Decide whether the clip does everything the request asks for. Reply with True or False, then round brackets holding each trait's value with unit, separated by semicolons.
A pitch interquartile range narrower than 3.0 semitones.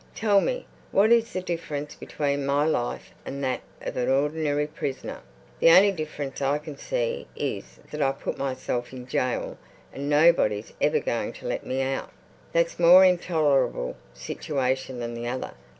False (4.2 semitones)